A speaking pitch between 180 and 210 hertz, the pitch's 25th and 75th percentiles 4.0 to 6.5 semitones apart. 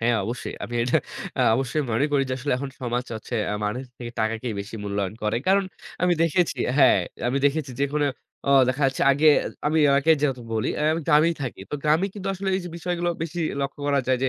No: medium, 140 Hz; average, 4.7 semitones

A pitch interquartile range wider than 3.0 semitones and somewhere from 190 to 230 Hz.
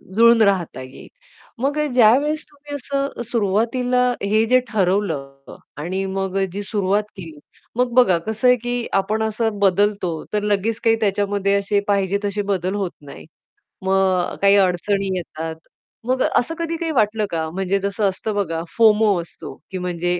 Yes: average, 3.5 semitones; high, 200 Hz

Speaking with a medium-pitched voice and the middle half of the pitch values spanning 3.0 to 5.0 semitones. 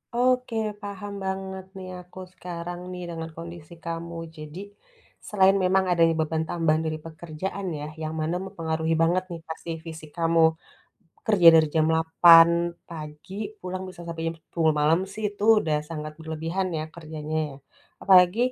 No: medium, 165 Hz; narrow, 2.6 semitones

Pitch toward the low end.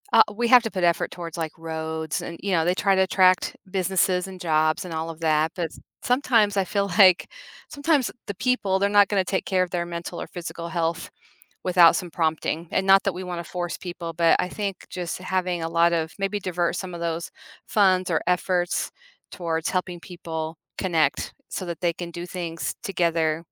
No: medium, 175 Hz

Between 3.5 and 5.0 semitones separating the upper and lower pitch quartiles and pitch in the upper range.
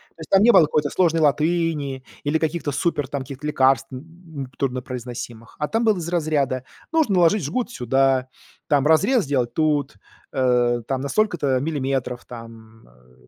No: average, 4.2 semitones; medium, 140 Hz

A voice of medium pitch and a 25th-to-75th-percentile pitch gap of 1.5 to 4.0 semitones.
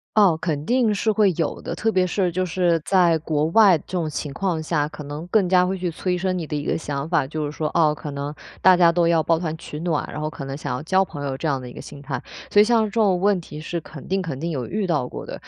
Yes: medium, 165 Hz; average, 3.7 semitones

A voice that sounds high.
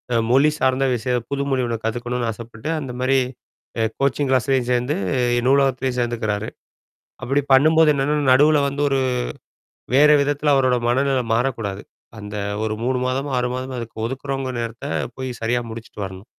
No: low, 130 Hz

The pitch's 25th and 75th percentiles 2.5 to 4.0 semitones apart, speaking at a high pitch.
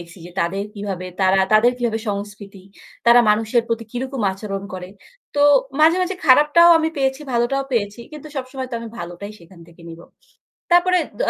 No: wide, 5.4 semitones; high, 225 Hz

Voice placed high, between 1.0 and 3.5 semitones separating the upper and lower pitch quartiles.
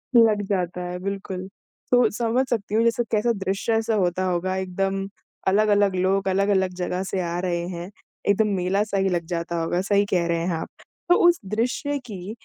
Yes: high, 195 Hz; average, 2.8 semitones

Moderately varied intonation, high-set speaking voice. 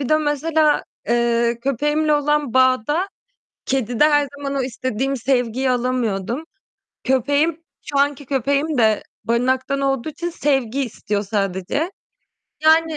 Yes: average, 3.7 semitones; very high, 270 Hz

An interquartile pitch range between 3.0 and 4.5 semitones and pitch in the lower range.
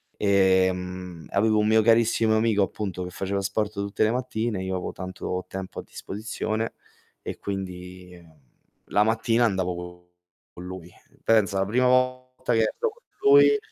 Yes: average, 3.4 semitones; low, 100 Hz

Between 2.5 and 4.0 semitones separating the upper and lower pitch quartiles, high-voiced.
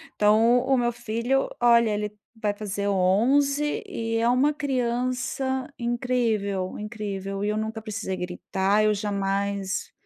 Yes: average, 3.5 semitones; high, 220 Hz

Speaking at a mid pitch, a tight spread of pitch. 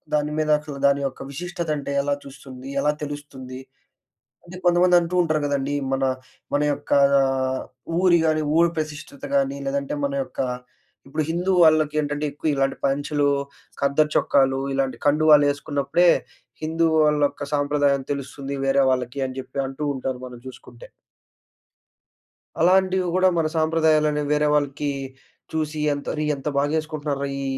Yes: medium, 145 Hz; narrow, 2.3 semitones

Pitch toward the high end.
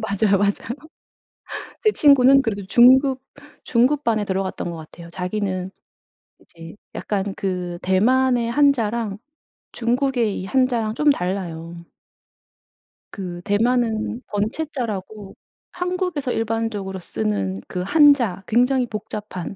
Yes: high, 215 Hz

